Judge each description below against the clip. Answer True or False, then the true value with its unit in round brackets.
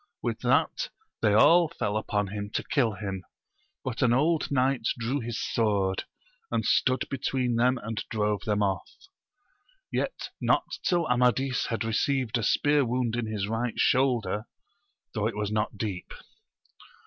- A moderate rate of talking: True (150 wpm)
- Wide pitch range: False (3.6 semitones)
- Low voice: True (115 Hz)